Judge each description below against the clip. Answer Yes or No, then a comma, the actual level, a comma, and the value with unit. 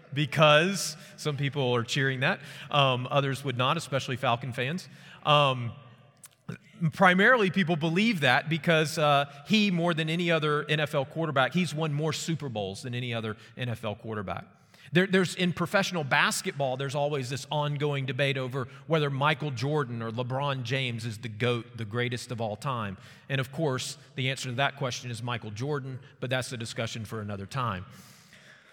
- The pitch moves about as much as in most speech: Yes, average, 3.8 semitones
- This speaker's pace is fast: No, average, 165 wpm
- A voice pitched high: No, medium, 140 Hz